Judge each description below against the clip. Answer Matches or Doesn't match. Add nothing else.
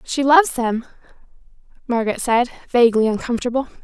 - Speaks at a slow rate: Matches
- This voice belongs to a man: Doesn't match